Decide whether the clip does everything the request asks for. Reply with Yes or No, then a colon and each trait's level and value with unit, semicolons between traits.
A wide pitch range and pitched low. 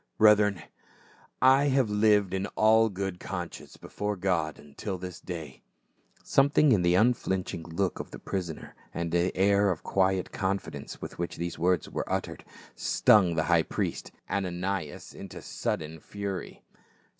No: average, 3.0 semitones; very low, 95 Hz